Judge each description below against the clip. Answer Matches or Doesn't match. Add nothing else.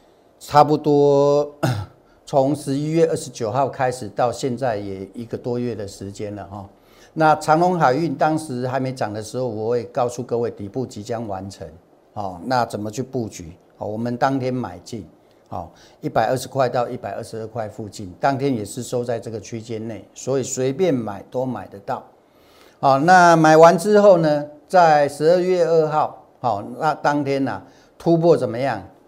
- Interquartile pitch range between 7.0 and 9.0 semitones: Doesn't match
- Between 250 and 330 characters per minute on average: Matches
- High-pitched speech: Doesn't match